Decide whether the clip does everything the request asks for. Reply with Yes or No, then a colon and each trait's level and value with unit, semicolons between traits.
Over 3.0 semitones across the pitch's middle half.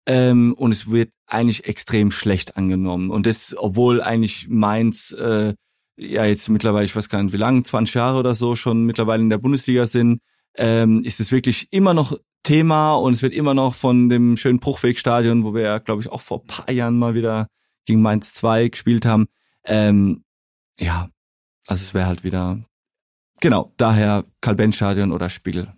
No: average, 2.7 semitones